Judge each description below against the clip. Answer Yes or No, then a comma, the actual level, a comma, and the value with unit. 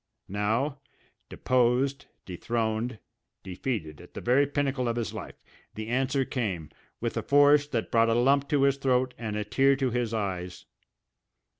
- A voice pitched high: No, low, 125 Hz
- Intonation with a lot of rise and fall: No, average, 3.8 semitones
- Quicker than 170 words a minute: No, average, 155 wpm